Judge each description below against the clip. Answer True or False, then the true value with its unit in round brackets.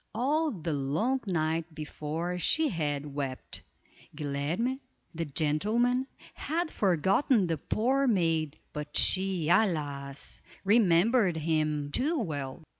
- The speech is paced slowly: True (110 wpm)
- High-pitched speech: False (170 Hz)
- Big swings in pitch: True (7.3 semitones)